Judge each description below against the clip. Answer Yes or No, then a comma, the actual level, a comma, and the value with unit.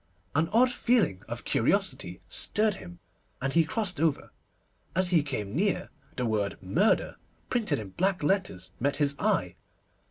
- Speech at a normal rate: Yes, average, 150 wpm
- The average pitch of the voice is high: No, medium, 160 Hz